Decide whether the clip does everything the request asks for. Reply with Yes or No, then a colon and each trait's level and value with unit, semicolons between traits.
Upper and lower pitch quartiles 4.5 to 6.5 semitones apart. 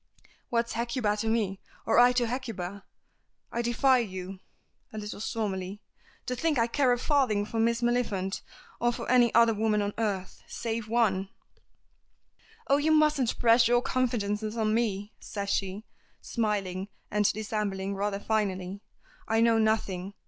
No: average, 3.0 semitones